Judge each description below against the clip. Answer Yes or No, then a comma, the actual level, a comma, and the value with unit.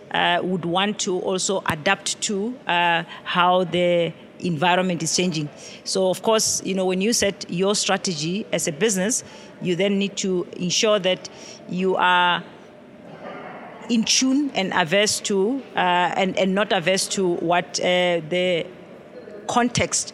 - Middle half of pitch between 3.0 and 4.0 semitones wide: No, narrow, 2.5 semitones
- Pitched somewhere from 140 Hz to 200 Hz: Yes, high, 190 Hz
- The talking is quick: No, average, 145 wpm